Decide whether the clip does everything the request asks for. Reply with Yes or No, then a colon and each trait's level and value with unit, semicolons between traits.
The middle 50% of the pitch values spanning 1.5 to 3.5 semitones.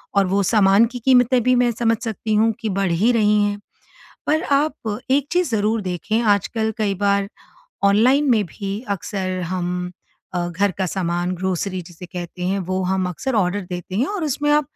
No: average, 4.0 semitones